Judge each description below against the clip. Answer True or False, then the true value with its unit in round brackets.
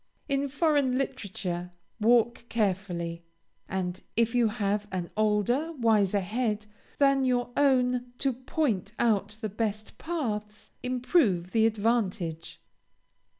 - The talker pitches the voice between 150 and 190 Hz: False (220 Hz)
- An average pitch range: True (4.1 semitones)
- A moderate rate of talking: False (110 wpm)